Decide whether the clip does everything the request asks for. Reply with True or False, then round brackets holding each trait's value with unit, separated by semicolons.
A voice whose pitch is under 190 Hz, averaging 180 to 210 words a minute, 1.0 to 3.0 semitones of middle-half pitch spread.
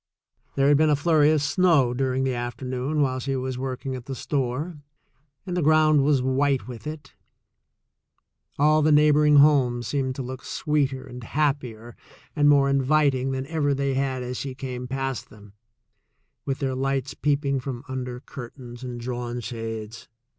False (135 Hz; 165 wpm; 2.5 semitones)